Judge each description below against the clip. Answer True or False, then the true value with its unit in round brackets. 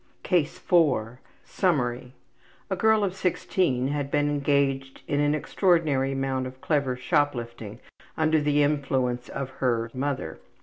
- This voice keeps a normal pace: False (130 wpm)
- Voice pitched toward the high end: False (140 Hz)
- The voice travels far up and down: False (2.9 semitones)